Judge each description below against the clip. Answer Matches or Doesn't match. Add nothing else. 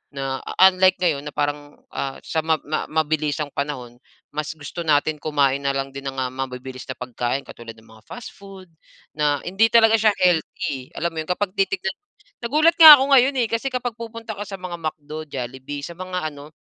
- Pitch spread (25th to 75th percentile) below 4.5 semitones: Doesn't match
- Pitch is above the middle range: Doesn't match